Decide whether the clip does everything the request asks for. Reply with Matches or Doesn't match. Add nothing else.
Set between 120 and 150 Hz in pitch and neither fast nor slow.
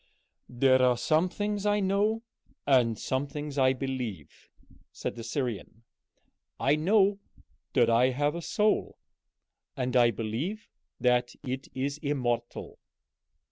Doesn't match